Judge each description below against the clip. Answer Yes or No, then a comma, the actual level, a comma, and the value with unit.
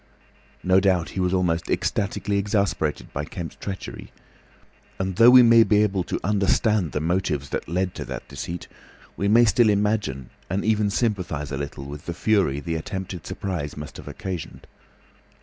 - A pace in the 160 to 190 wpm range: Yes, average, 165 wpm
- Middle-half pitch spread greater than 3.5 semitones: Yes, average, 3.9 semitones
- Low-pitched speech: Yes, very low, 95 Hz